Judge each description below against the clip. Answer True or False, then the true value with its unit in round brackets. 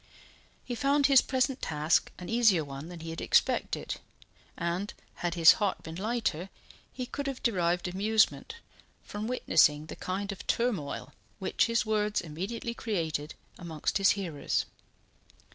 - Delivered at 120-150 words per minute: True (145 wpm)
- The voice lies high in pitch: True (195 Hz)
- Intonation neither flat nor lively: False (6.0 semitones)